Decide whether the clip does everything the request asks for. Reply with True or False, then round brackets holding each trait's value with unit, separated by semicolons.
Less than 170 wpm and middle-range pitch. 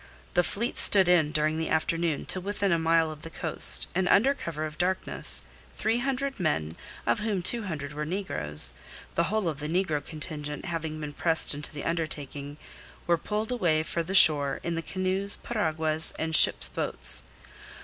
False (180 wpm; 165 Hz)